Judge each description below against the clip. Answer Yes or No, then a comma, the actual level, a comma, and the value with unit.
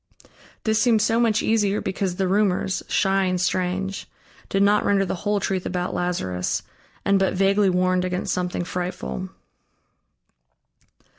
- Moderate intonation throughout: No, narrow, 2.0 semitones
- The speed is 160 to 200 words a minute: No, average, 140 wpm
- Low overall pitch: No, high, 190 Hz